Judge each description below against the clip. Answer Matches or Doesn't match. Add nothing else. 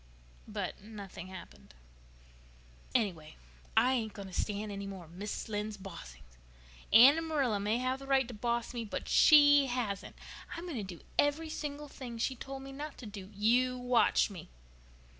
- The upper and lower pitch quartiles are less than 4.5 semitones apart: Doesn't match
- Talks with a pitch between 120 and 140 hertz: Doesn't match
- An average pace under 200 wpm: Matches